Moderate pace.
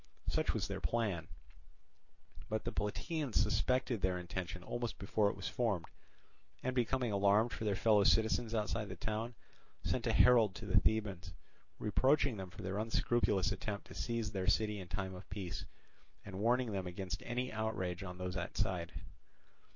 Yes: average, 165 wpm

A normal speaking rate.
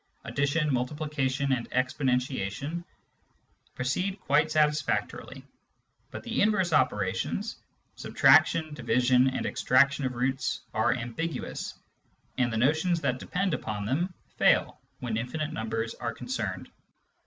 No: slow, 120 wpm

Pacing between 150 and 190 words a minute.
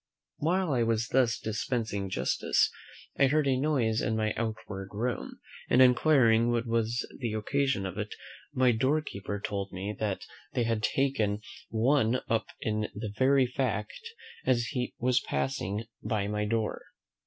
Yes: average, 155 wpm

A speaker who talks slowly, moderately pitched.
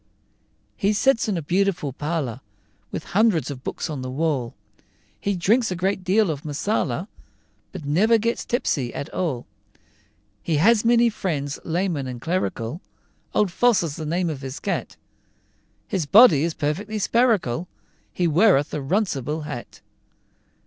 No: average, 150 wpm; medium, 170 Hz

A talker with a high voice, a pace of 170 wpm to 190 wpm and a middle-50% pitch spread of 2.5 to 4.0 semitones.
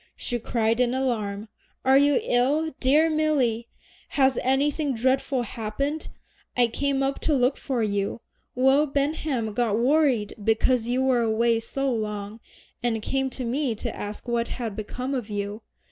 No: very high, 250 Hz; average, 155 wpm; average, 3.4 semitones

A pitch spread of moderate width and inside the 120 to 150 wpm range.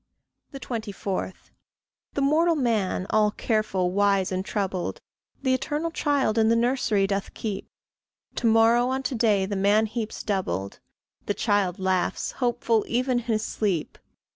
Yes: average, 3.7 semitones; average, 140 wpm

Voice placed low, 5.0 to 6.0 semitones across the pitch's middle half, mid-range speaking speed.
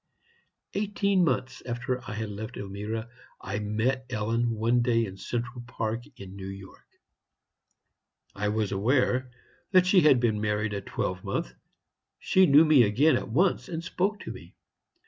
No: low, 115 Hz; average, 4.2 semitones; average, 155 wpm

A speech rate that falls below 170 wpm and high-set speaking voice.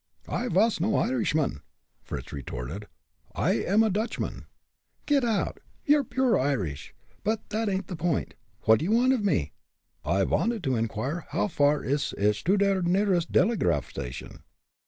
No: average, 155 wpm; medium, 180 Hz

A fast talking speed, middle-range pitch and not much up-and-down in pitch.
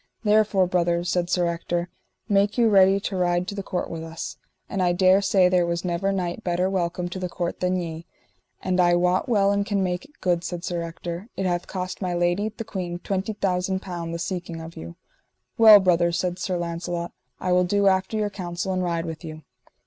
Yes: fast, 215 wpm; medium, 180 Hz; narrow, 1.9 semitones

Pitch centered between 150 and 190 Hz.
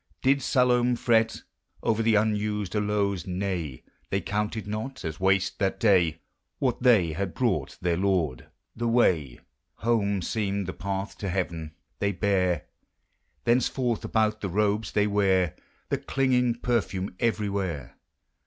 No: low, 100 Hz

